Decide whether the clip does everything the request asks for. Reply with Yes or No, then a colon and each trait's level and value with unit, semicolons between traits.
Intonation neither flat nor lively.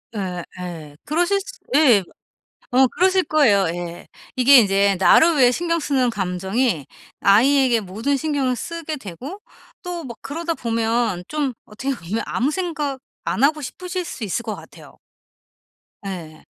No: wide, 7.4 semitones